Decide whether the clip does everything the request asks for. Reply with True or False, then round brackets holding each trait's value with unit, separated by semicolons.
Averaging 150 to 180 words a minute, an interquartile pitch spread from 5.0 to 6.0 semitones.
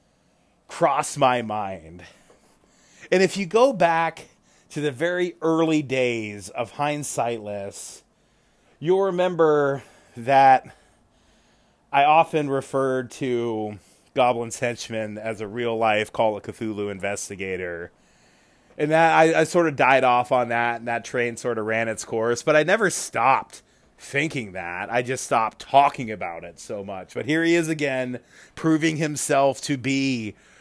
False (140 wpm; 5.5 semitones)